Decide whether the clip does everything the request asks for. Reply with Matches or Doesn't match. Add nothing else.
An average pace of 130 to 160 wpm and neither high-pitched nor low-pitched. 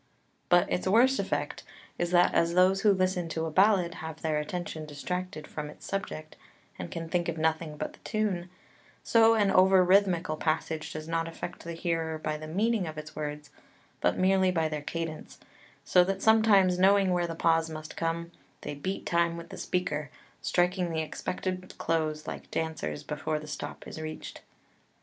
Doesn't match